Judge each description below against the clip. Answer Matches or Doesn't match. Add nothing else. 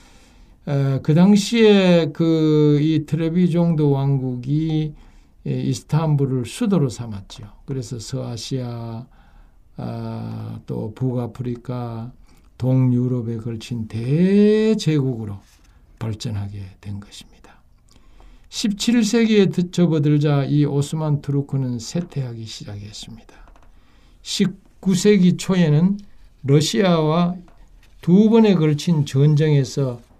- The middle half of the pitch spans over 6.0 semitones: Matches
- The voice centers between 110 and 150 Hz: Matches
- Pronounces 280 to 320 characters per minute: Doesn't match